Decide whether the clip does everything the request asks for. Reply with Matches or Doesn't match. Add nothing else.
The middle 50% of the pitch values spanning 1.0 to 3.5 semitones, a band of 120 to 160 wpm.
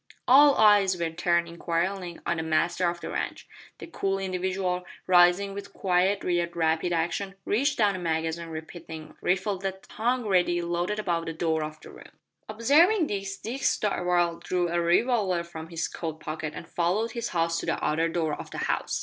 Doesn't match